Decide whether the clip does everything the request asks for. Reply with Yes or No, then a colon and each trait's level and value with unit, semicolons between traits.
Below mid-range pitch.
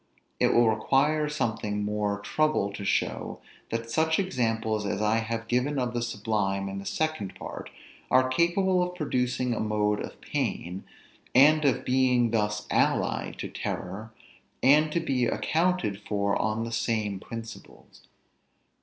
Yes: low, 115 Hz